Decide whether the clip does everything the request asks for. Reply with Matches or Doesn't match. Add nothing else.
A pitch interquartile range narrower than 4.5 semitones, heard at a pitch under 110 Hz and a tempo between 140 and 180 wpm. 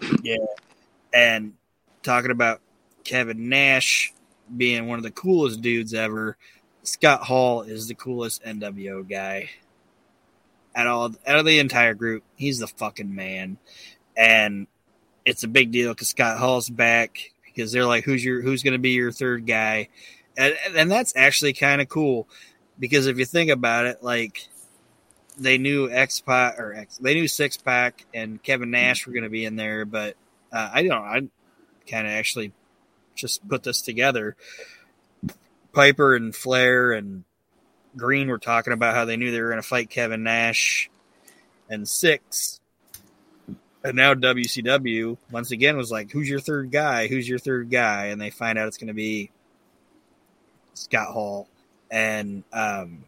Doesn't match